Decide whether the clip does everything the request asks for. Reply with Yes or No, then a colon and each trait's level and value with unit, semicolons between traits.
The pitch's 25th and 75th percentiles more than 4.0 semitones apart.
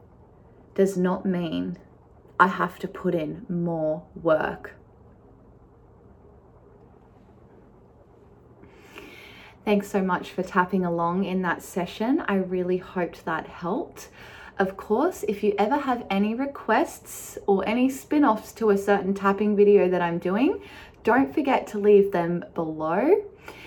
No: average, 3.3 semitones